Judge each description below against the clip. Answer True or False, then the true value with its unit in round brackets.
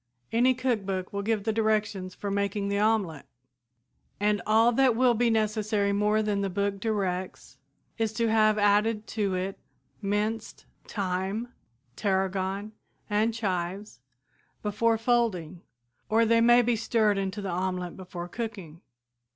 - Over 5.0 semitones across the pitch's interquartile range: False (2.6 semitones)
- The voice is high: True (210 Hz)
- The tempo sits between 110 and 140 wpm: True (135 wpm)